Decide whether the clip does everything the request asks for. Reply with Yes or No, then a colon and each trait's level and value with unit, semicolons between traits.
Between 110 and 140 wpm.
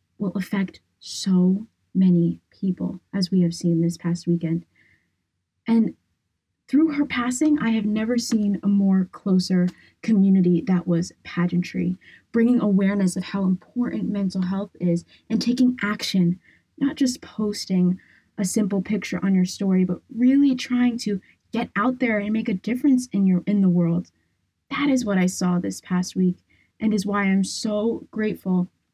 No: average, 160 wpm